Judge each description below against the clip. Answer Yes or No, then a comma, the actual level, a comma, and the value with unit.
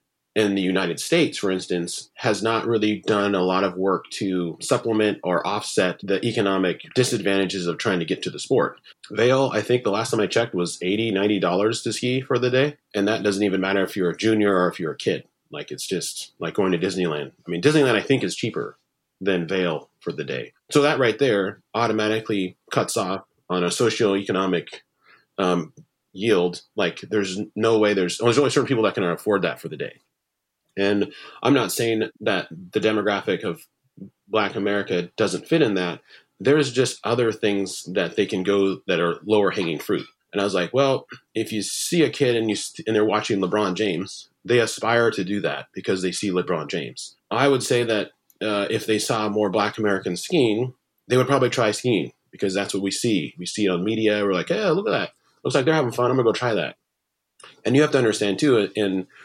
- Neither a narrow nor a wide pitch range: Yes, average, 3.0 semitones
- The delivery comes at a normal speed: No, fast, 215 wpm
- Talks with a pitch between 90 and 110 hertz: Yes, low, 105 Hz